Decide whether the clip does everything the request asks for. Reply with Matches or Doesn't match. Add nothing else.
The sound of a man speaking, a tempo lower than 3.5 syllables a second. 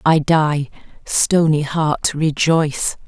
Doesn't match